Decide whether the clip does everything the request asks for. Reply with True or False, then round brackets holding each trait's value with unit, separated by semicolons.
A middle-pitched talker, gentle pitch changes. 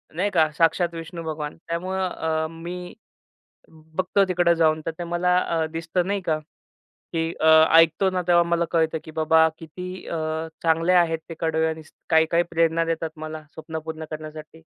True (165 Hz; 1.5 semitones)